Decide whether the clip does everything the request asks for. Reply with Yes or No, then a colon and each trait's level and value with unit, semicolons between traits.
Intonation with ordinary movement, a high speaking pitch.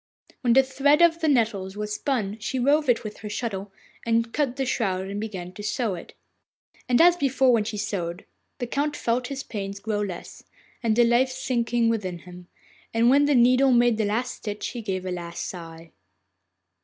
Yes: average, 4.4 semitones; high, 230 Hz